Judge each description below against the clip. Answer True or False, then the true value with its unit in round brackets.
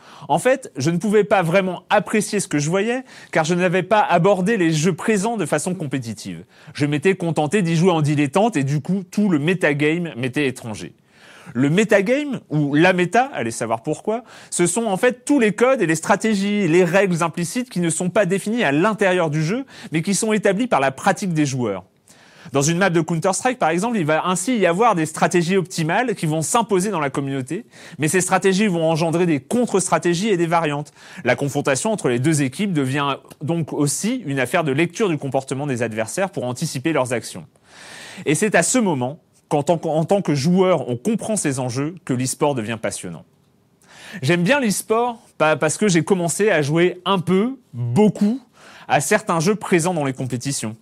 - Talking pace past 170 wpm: True (195 wpm)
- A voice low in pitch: False (175 Hz)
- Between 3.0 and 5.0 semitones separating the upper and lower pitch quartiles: False (5.5 semitones)